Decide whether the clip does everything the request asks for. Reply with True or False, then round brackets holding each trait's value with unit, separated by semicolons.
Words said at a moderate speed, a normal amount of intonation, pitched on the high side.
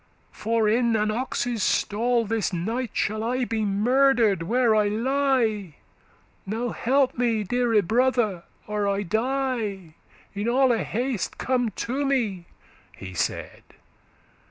False (125 wpm; 3.2 semitones; 225 Hz)